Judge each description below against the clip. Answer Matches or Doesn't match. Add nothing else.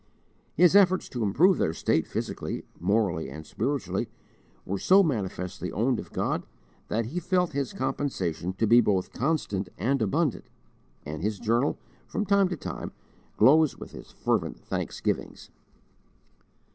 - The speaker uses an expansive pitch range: Matches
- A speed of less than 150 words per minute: Matches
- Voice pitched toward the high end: Doesn't match